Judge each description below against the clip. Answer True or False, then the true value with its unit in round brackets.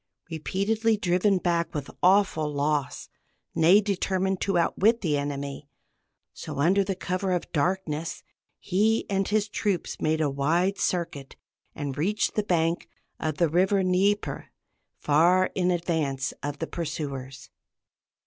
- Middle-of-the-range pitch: True (175 Hz)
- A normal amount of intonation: True (4.4 semitones)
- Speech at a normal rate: False (130 wpm)